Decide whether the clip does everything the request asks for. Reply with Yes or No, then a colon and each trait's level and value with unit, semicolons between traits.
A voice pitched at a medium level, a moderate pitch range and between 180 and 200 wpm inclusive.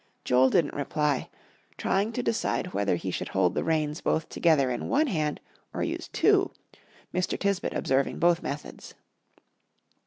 No: medium, 155 Hz; average, 5.0 semitones; average, 150 wpm